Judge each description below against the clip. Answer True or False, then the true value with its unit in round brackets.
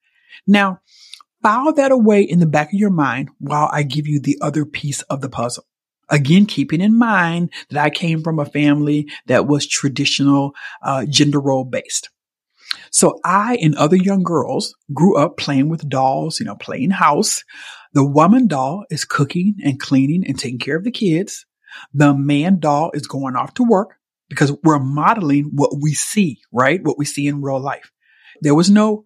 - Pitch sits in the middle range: True (150 Hz)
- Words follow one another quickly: False (185 wpm)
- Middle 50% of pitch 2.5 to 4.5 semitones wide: False (5.5 semitones)